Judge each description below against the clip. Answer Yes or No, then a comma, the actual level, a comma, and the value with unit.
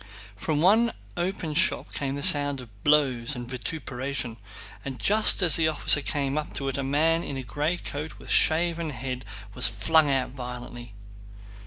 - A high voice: No, medium, 140 Hz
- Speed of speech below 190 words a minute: Yes, average, 175 wpm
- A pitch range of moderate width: Yes, average, 3.9 semitones